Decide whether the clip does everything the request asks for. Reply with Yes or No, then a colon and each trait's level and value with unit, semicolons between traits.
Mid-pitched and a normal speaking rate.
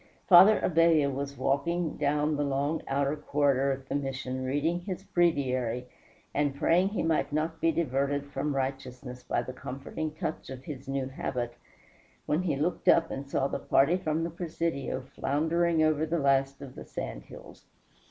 Yes: medium, 145 Hz; average, 170 wpm